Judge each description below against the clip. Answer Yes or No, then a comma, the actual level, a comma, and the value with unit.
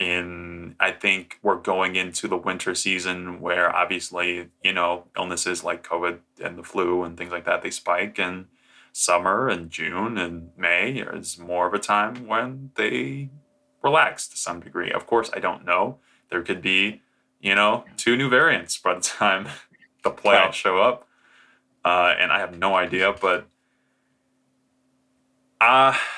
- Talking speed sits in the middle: Yes, average, 165 wpm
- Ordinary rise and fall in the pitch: No, wide, 6.5 semitones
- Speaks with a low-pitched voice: Yes, very low, 95 Hz